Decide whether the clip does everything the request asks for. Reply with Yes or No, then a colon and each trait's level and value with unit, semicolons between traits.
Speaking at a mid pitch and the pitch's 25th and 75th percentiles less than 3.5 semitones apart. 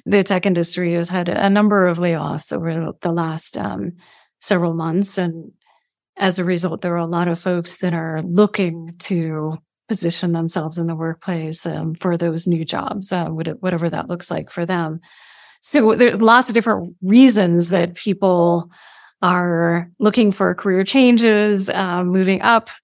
Yes: medium, 180 Hz; average, 2.7 semitones